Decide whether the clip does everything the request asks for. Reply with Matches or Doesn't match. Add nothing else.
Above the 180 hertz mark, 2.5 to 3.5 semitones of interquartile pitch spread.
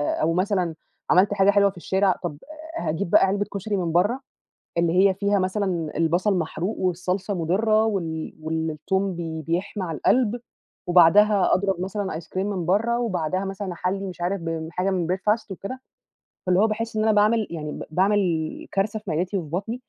Matches